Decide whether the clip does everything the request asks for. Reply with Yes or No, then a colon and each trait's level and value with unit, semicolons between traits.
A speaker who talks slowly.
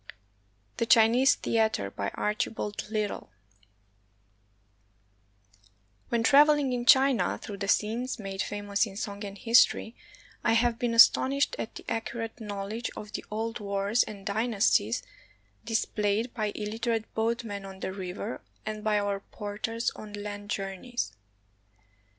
Yes: slow, 125 wpm